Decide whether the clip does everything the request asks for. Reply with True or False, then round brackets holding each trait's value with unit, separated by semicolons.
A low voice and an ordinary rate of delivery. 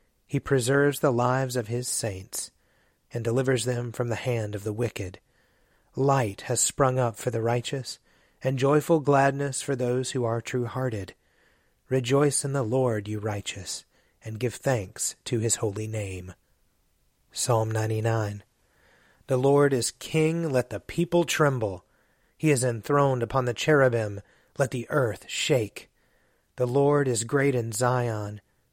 True (125 Hz; 150 wpm)